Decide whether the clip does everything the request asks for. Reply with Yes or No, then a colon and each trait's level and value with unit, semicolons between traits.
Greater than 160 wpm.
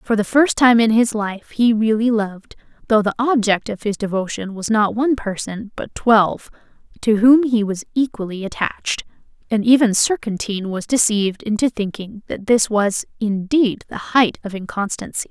Yes: average, 170 wpm